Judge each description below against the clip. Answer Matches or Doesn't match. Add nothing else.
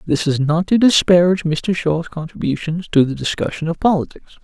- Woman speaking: Doesn't match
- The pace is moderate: Matches